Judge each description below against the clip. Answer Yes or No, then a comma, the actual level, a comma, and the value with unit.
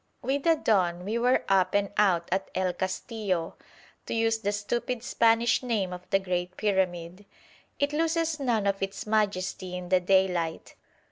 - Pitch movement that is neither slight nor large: Yes, average, 3.9 semitones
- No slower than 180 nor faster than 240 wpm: No, average, 160 wpm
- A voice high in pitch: Yes, high, 195 Hz